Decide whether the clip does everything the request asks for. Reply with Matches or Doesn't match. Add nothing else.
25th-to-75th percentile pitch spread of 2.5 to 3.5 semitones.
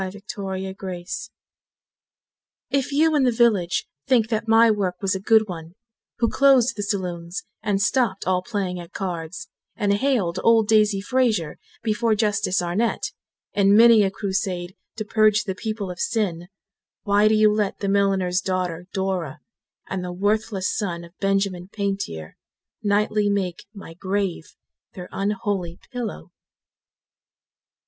Matches